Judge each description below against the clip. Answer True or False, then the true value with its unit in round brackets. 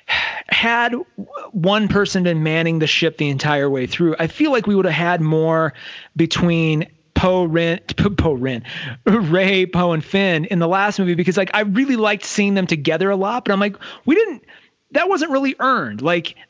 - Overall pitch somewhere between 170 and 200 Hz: True (185 Hz)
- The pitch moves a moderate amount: True (4.2 semitones)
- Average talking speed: True (180 wpm)